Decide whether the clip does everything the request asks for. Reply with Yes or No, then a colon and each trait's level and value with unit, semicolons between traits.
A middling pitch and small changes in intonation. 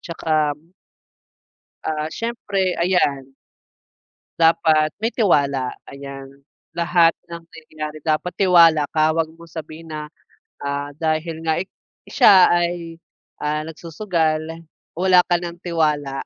Yes: medium, 160 Hz; narrow, 2.1 semitones